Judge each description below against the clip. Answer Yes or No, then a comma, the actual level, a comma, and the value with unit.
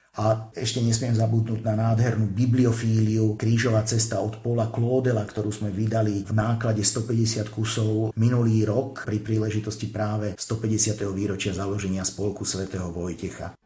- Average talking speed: Yes, average, 130 wpm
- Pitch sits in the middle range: No, low, 110 Hz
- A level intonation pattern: Yes, narrow, 1.4 semitones